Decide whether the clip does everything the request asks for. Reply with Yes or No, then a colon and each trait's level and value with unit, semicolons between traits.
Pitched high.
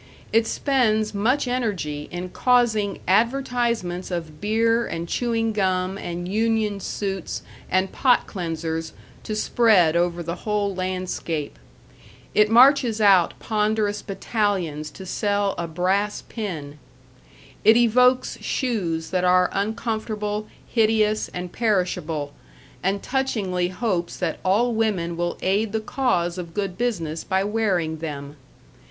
Yes: high, 200 Hz